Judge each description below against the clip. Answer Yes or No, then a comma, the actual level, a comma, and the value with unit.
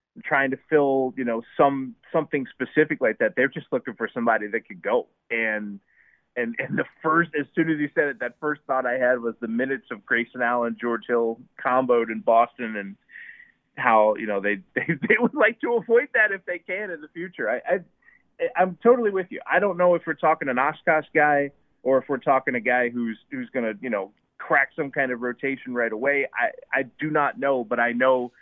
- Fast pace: Yes, fast, 220 wpm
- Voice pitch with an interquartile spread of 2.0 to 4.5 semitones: No, average, 5.0 semitones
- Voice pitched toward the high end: No, low, 135 Hz